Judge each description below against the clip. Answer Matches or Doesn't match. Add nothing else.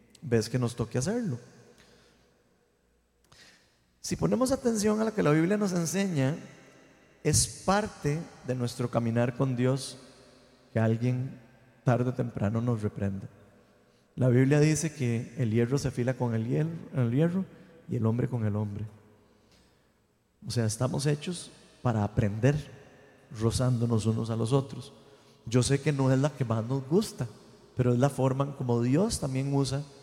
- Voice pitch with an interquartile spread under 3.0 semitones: Doesn't match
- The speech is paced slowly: Doesn't match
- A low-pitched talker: Matches